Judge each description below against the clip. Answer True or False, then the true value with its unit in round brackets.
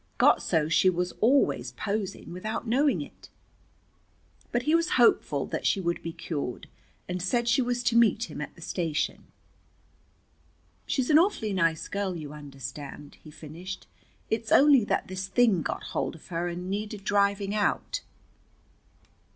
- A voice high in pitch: True (195 Hz)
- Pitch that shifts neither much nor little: False (5.9 semitones)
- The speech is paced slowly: False (155 wpm)